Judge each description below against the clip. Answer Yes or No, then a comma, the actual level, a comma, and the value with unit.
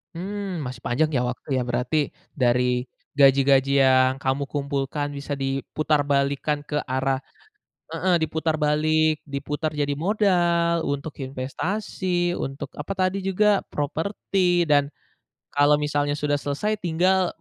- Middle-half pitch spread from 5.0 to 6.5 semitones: No, average, 3.8 semitones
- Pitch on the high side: No, medium, 145 Hz